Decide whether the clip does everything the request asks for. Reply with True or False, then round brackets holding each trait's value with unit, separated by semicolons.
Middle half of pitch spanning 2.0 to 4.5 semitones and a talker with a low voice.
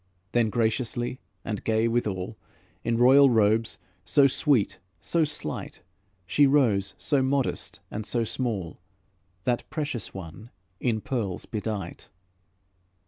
True (3.8 semitones; 115 Hz)